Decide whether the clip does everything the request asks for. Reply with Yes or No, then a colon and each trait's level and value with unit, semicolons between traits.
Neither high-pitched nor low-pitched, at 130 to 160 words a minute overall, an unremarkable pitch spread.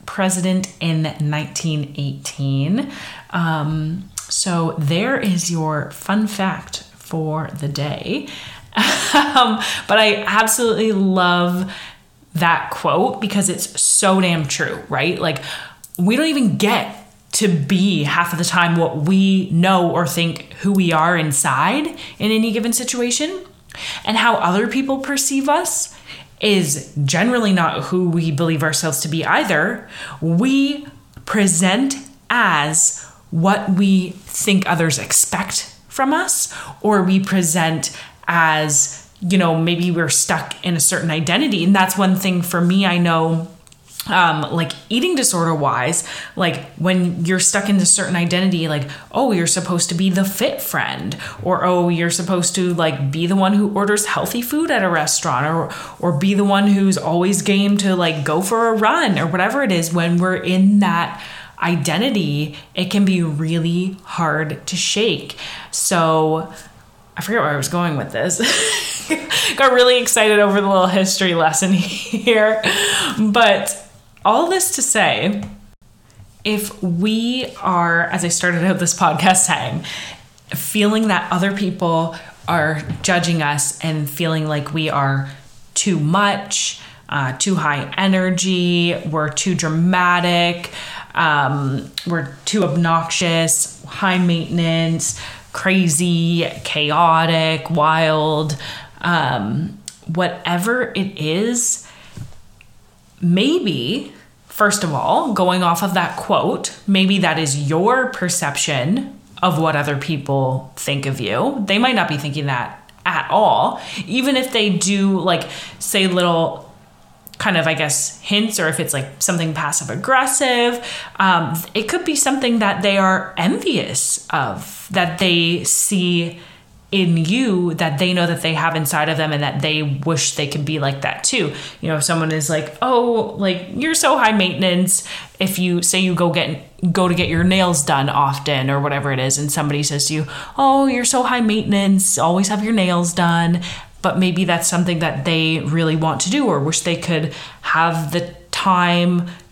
Yes: medium, 175 Hz; average, 150 wpm; average, 3.7 semitones